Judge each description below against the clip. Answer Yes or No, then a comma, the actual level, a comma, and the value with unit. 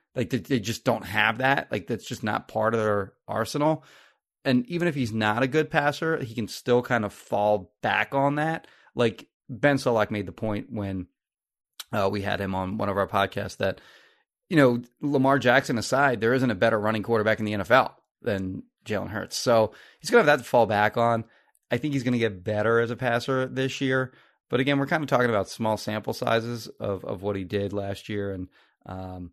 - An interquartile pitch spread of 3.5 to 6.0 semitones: Yes, average, 4.2 semitones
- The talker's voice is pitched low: Yes, low, 115 Hz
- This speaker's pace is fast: Yes, fast, 215 wpm